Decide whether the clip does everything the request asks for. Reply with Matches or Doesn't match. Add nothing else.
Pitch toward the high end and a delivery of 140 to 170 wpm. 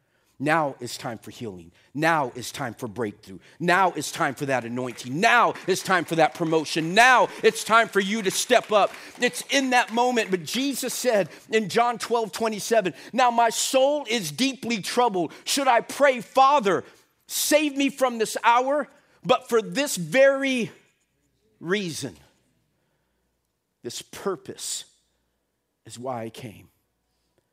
Matches